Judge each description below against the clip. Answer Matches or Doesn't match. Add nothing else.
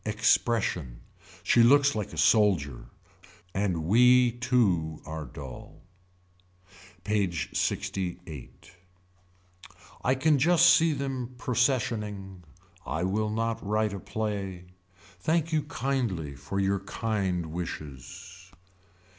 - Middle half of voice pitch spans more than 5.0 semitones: Matches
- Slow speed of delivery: Matches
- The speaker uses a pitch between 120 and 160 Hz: Doesn't match